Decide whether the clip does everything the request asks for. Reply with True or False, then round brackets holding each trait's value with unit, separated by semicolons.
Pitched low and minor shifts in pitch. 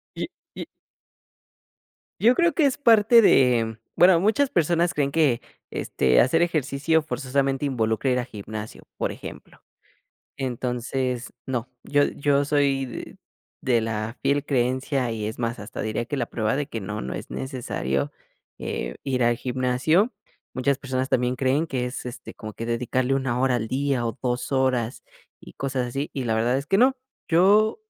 False (130 Hz; 3.3 semitones)